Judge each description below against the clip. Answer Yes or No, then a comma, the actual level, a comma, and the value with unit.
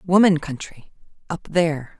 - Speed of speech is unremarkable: No, slow, 90 wpm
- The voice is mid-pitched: Yes, medium, 165 Hz